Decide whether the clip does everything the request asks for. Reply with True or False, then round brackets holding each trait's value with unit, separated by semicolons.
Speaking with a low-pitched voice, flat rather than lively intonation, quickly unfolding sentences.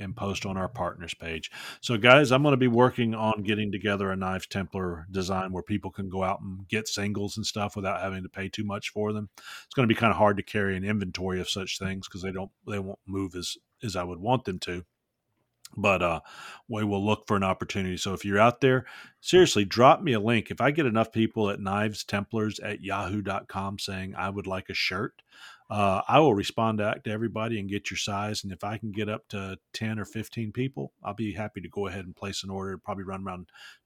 True (100 Hz; 2.2 semitones; 235 wpm)